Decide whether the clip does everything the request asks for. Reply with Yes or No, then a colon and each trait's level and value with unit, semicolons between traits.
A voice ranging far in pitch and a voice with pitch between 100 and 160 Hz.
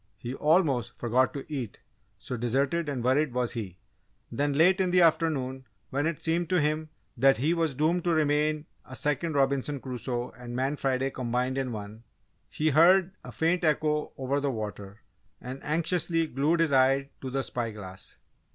No: average, 3.8 semitones; medium, 140 Hz